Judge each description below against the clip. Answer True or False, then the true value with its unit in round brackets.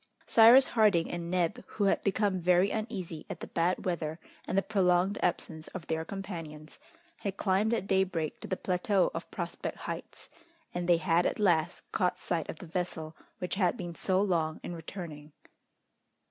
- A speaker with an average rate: True (175 wpm)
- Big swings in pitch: False (2.7 semitones)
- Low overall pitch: False (180 Hz)